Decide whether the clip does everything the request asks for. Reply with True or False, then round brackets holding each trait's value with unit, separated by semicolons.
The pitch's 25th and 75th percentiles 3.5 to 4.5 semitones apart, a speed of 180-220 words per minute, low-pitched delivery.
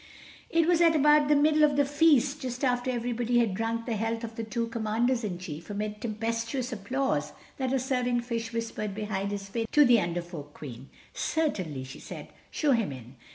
False (4.2 semitones; 200 wpm; 230 Hz)